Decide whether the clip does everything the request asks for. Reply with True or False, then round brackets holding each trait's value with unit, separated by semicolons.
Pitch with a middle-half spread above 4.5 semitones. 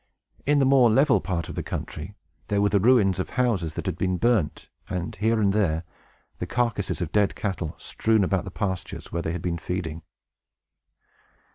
False (4.2 semitones)